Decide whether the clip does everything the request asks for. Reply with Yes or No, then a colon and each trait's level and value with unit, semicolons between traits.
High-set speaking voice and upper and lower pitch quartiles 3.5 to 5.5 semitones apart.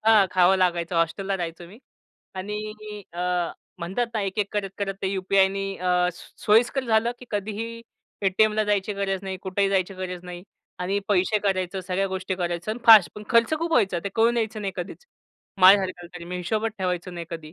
No: high, 195 Hz; average, 2.8 semitones